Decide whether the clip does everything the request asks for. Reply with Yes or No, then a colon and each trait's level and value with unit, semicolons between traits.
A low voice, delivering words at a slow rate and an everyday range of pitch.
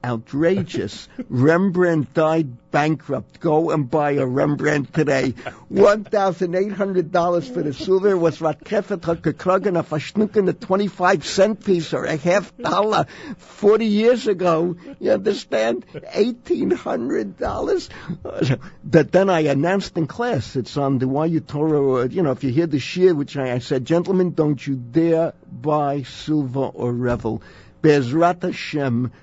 No: medium, 160 Hz; slow, 125 wpm; average, 4.9 semitones